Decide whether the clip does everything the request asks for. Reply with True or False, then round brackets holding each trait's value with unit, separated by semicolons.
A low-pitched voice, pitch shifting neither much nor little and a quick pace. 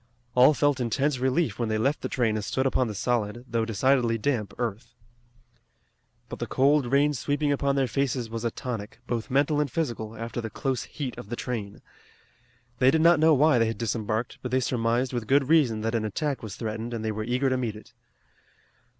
True (125 Hz; 3.5 semitones; 210 wpm)